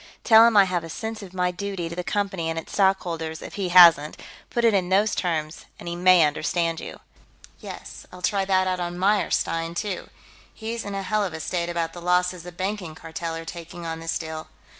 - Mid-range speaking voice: Yes, medium, 180 Hz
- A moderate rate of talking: No, fast, 220 wpm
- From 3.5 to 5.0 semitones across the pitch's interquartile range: No, average, 2.8 semitones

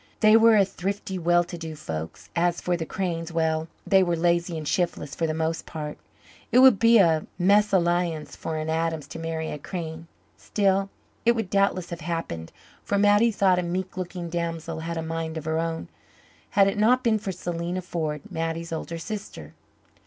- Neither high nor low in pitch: Yes, medium, 170 Hz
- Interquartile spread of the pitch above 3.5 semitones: No, average, 3.1 semitones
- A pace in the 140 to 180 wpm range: No, average, 190 wpm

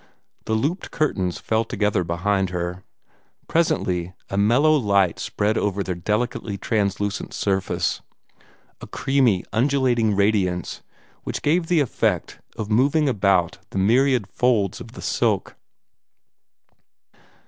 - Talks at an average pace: No, slow, 120 wpm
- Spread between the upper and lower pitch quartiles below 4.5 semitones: No, average, 4.8 semitones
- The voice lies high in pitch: No, low, 105 Hz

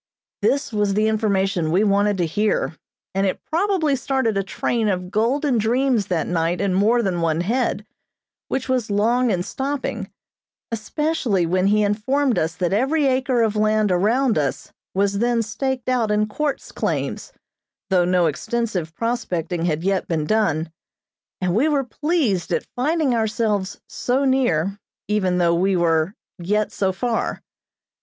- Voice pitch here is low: No, high, 210 Hz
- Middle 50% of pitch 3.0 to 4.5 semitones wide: No, average, 5.2 semitones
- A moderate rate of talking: Yes, average, 155 wpm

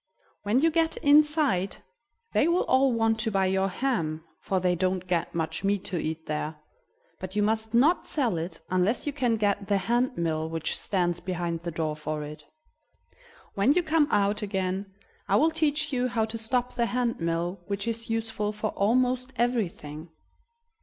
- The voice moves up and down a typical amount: No, wide, 5.9 semitones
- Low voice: No, high, 205 Hz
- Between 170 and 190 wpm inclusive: Yes, average, 180 wpm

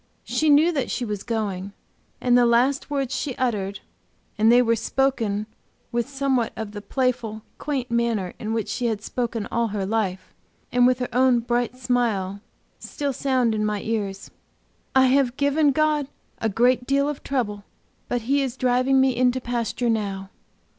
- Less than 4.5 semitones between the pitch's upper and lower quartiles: Yes, average, 3.3 semitones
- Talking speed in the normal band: Yes, average, 170 wpm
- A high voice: Yes, high, 240 Hz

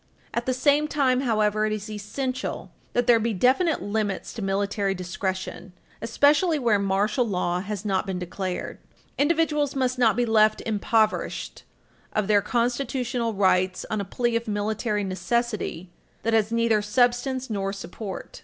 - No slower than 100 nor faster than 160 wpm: Yes, average, 150 wpm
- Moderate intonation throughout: Yes, average, 3.7 semitones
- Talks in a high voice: Yes, high, 220 Hz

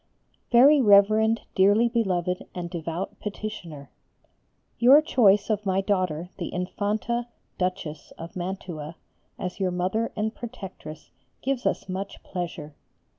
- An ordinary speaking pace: No, slow, 125 wpm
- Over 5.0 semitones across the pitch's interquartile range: No, average, 3.7 semitones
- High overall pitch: Yes, high, 195 Hz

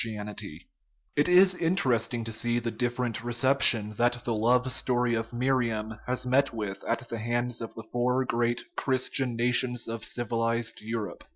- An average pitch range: No, narrow, 1.7 semitones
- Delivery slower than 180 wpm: Yes, average, 160 wpm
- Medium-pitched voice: No, low, 120 Hz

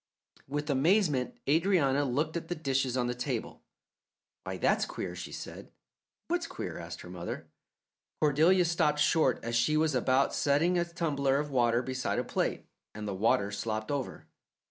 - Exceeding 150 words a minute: Yes, average, 165 wpm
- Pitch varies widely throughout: No, average, 4.2 semitones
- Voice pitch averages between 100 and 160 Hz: Yes, medium, 140 Hz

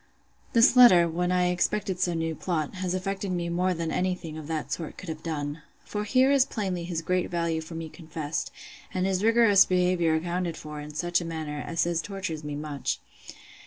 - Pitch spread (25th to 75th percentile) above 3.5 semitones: No, narrow, 2.5 semitones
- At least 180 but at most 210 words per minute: Yes, average, 200 wpm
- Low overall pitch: No, medium, 175 Hz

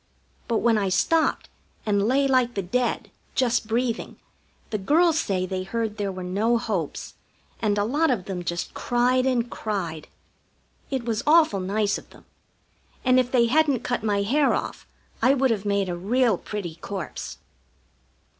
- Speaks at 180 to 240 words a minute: No, average, 165 wpm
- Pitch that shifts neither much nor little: Yes, average, 4.4 semitones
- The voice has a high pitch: Yes, high, 225 Hz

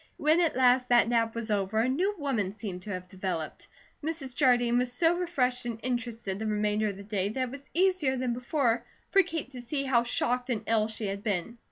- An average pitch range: Yes, average, 3.9 semitones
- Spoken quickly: Yes, fast, 220 wpm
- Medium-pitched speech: No, high, 240 Hz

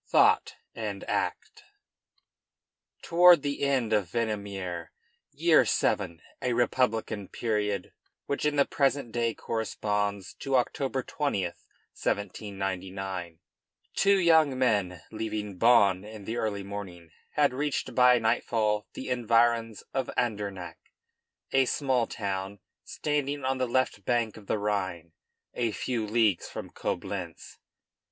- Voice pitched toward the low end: Yes, low, 110 Hz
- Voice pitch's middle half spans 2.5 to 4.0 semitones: No, average, 4.4 semitones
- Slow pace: Yes, slow, 120 wpm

